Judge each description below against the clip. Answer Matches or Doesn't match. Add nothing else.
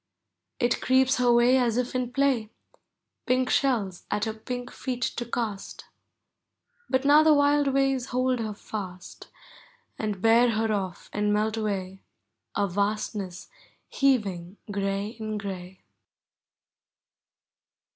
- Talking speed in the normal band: Doesn't match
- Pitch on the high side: Matches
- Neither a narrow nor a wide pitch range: Matches